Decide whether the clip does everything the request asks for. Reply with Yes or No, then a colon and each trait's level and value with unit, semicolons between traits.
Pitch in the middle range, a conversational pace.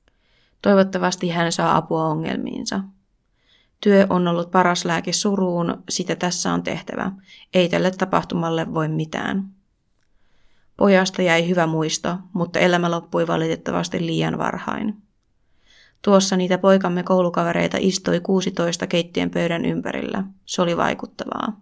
Yes: medium, 180 Hz; average, 115 wpm